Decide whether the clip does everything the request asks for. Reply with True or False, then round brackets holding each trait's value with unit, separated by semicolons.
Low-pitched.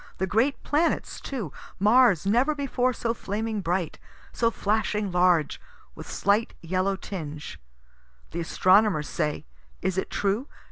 False (200 Hz)